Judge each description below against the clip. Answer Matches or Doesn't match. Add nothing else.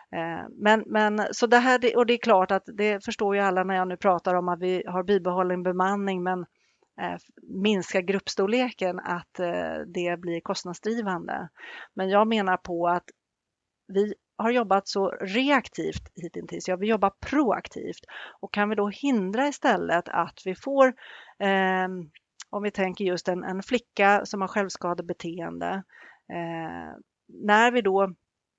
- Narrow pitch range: Doesn't match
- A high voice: Matches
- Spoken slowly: Doesn't match